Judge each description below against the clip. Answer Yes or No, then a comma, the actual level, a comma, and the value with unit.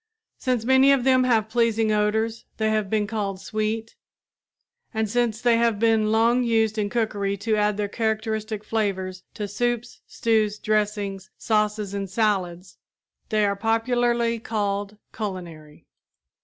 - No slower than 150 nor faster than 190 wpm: No, average, 140 wpm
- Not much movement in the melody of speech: Yes, narrow, 1.9 semitones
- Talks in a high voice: Yes, high, 215 Hz